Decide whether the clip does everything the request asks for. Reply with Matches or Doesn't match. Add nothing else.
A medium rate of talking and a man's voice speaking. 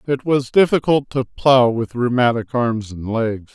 Matches